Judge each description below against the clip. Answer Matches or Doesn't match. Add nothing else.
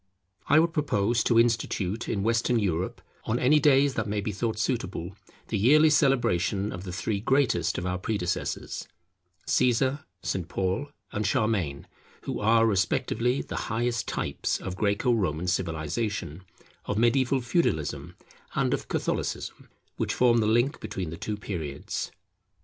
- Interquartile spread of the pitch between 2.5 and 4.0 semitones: Doesn't match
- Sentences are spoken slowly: Doesn't match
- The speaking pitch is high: Doesn't match